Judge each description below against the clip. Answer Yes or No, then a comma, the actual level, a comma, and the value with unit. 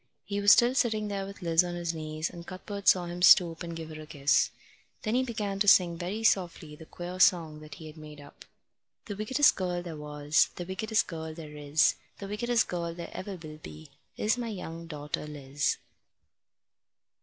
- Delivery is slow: No, average, 200 wpm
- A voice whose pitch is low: No, medium, 175 Hz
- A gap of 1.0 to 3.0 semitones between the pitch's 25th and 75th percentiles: No, average, 4.4 semitones